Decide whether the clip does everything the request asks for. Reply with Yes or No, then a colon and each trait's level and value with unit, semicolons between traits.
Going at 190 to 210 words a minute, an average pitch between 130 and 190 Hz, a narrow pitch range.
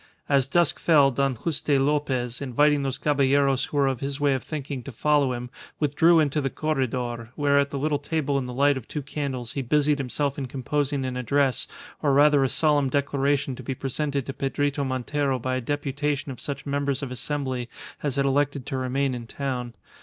Yes: average, 200 wpm; medium, 140 Hz; narrow, 1.9 semitones